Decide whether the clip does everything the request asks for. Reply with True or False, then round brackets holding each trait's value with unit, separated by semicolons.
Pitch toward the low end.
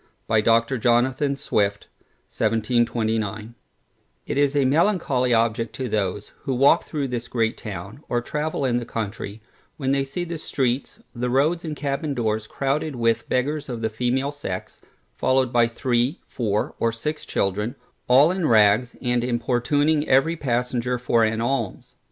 True (125 Hz)